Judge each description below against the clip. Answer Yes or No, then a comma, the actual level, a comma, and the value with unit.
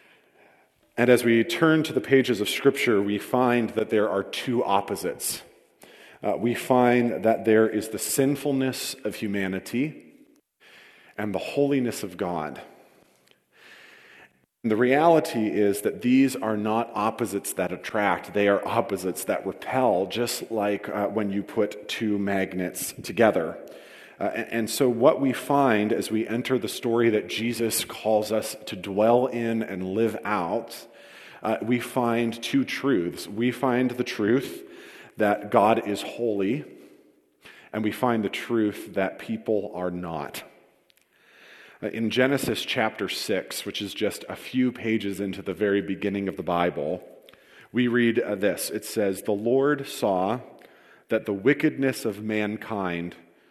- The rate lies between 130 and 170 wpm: Yes, average, 150 wpm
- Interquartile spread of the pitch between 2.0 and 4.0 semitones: Yes, average, 3.5 semitones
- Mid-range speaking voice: No, low, 115 Hz